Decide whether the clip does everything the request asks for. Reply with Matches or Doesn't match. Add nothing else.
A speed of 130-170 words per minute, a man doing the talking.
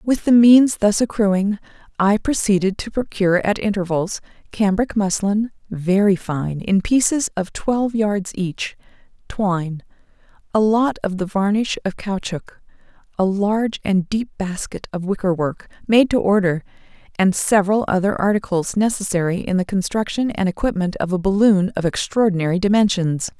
Doesn't match